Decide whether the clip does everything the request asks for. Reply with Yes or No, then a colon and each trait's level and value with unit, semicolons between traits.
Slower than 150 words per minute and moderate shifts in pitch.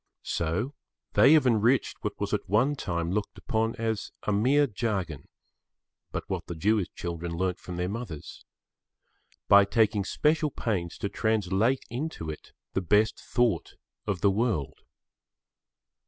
Yes: slow, 135 wpm; average, 4.8 semitones